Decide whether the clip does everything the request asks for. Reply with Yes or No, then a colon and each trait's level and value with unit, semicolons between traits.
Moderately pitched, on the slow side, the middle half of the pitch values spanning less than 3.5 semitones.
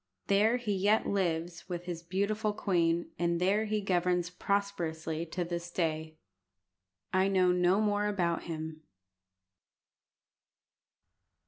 Yes: medium, 180 Hz; slow, 115 wpm; average, 3.0 semitones